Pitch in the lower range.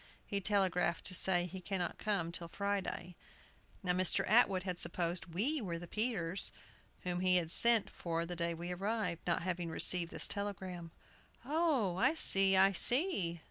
No: medium, 185 Hz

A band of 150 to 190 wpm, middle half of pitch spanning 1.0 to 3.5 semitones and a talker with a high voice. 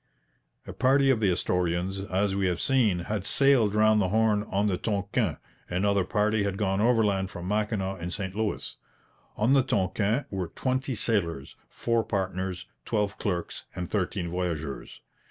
No: average, 155 wpm; average, 2.9 semitones; low, 100 Hz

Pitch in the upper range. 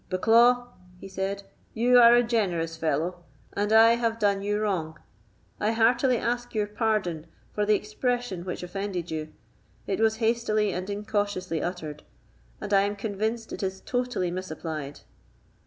Yes: high, 205 Hz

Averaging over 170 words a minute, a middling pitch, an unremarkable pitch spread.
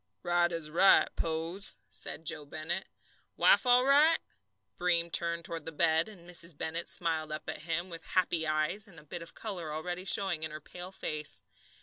No: average, 190 wpm; medium, 170 Hz; narrow, 2.2 semitones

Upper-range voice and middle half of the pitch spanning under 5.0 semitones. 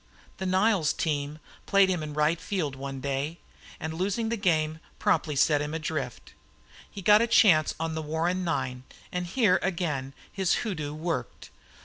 No: medium, 160 Hz; average, 3.8 semitones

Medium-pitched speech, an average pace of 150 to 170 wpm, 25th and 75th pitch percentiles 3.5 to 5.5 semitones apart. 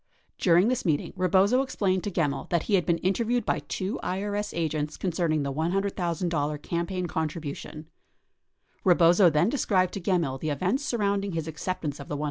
Yes: medium, 175 Hz; average, 165 wpm; average, 3.9 semitones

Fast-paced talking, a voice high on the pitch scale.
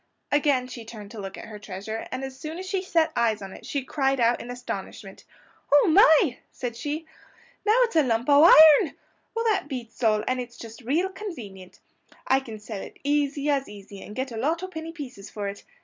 Yes: fast, 220 wpm; very high, 255 Hz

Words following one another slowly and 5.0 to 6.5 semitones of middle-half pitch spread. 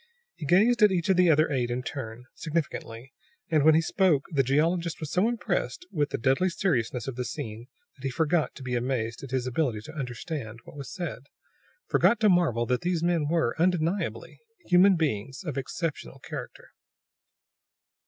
No: average, 180 wpm; wide, 5.6 semitones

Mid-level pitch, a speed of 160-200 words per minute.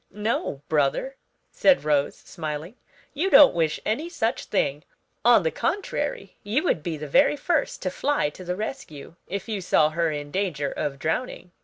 Yes: medium, 180 Hz; average, 170 wpm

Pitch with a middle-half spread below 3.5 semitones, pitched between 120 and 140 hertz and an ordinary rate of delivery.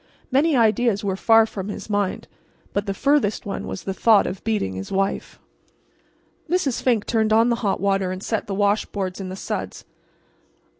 No: average, 2.7 semitones; high, 205 Hz; average, 180 wpm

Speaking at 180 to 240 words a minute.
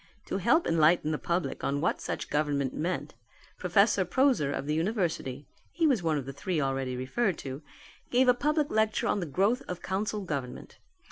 Yes: average, 190 wpm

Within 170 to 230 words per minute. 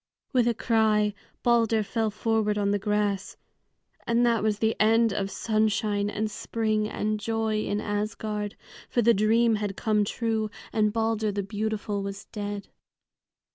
No: average, 150 wpm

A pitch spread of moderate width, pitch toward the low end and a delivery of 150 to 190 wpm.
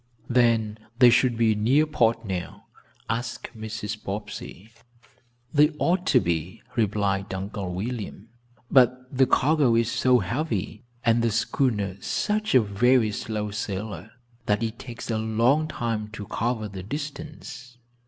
No: average, 3.4 semitones; low, 115 Hz; slow, 135 wpm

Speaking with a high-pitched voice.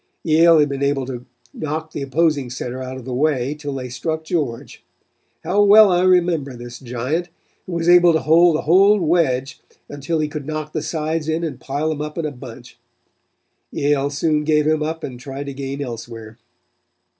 No: medium, 150 Hz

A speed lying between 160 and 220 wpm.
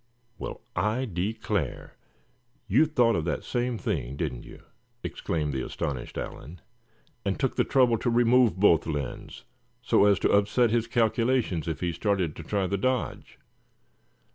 No: average, 150 wpm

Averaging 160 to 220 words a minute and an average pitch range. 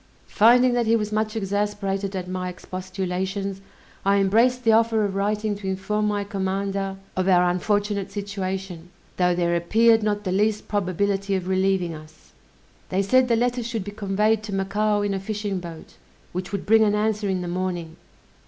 No: average, 175 wpm; narrow, 2.2 semitones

